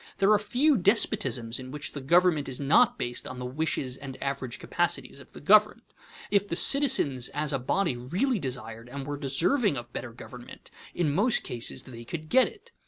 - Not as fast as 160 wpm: No, average, 190 wpm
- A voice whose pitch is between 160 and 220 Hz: No, medium, 145 Hz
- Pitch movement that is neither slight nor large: No, wide, 7.7 semitones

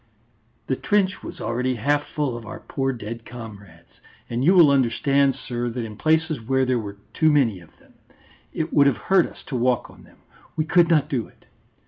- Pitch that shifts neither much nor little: Yes, average, 4.3 semitones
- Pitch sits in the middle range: No, low, 130 Hz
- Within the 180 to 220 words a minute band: Yes, average, 200 wpm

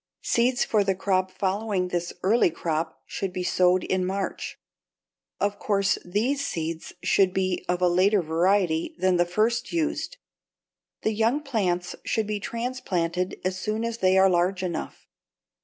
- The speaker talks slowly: No, average, 155 wpm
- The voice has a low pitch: No, high, 190 Hz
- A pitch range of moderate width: Yes, average, 3.3 semitones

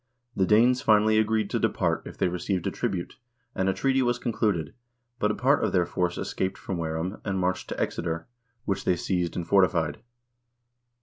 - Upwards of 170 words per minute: Yes, average, 190 wpm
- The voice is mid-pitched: No, very low, 95 Hz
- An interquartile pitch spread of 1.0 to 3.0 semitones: No, average, 3.6 semitones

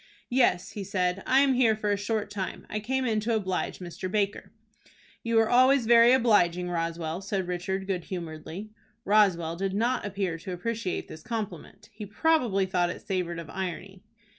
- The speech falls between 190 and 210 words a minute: No, average, 175 wpm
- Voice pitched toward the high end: Yes, high, 195 Hz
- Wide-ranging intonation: No, average, 3.9 semitones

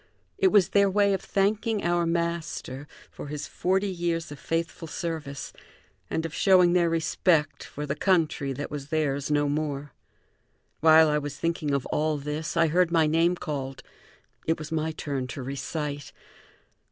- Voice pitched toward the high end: No, medium, 160 Hz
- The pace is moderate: Yes, average, 165 wpm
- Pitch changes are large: No, average, 2.8 semitones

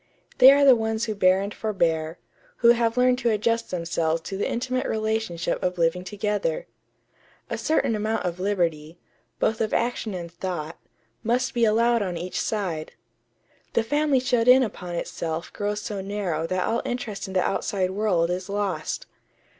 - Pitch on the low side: No, high, 205 Hz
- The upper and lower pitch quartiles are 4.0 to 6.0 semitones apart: Yes, average, 4.5 semitones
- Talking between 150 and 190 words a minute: Yes, average, 170 wpm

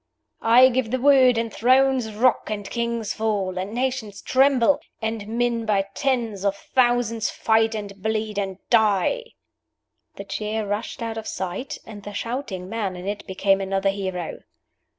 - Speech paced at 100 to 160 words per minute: Yes, average, 155 wpm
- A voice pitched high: Yes, high, 220 Hz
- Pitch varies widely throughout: No, average, 3.3 semitones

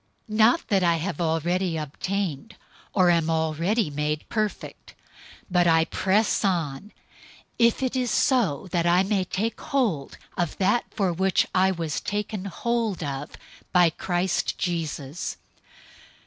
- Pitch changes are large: No, average, 4.1 semitones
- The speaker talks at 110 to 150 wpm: Yes, average, 140 wpm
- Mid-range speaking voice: Yes, medium, 180 Hz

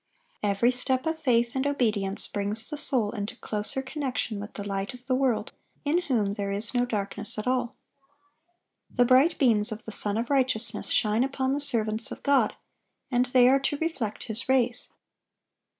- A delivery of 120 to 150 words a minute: No, average, 180 wpm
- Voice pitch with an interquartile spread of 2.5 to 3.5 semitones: No, average, 3.9 semitones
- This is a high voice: Yes, high, 245 Hz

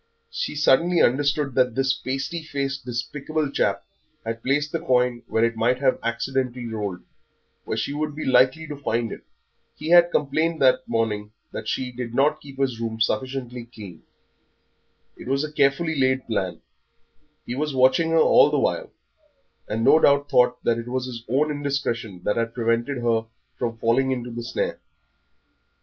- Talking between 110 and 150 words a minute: No, average, 170 wpm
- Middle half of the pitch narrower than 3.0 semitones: No, average, 3.5 semitones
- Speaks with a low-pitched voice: Yes, low, 130 Hz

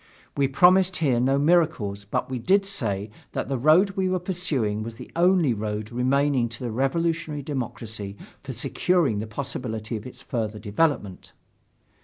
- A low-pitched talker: Yes, low, 130 Hz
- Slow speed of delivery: No, average, 160 wpm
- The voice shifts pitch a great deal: Yes, wide, 7.2 semitones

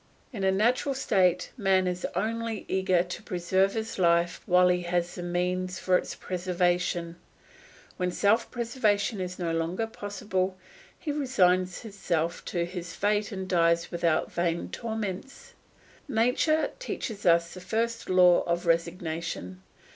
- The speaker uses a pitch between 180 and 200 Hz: Yes, medium, 185 Hz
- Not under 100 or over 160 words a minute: Yes, average, 140 wpm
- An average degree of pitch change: Yes, average, 3.4 semitones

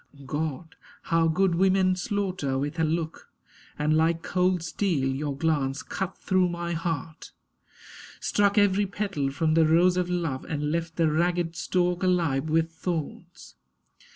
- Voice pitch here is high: No, medium, 165 Hz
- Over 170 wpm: No, average, 145 wpm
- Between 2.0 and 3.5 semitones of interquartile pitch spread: Yes, narrow, 2.6 semitones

